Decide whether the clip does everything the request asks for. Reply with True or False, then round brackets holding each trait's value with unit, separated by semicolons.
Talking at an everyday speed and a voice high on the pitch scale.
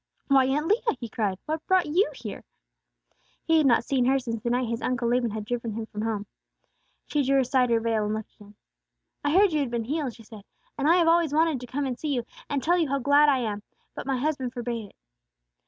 False (245 wpm; 255 Hz)